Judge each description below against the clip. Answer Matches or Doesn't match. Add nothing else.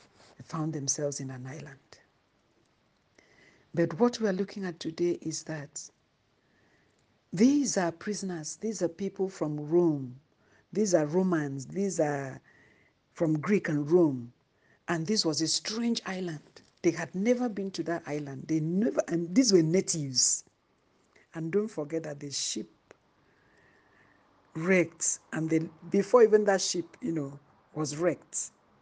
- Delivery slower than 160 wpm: Matches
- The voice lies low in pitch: Doesn't match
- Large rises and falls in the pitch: Doesn't match